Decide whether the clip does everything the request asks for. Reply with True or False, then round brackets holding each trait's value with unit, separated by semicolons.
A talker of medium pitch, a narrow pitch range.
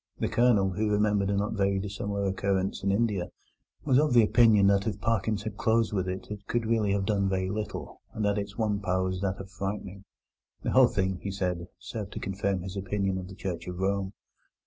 False (100 Hz; 1.7 semitones)